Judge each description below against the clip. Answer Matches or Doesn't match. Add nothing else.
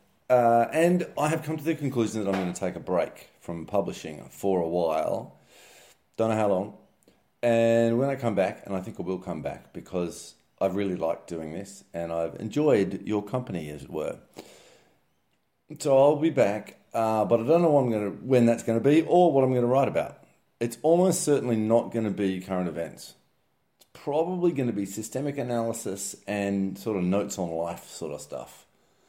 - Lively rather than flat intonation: Matches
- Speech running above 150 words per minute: Matches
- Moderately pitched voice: Doesn't match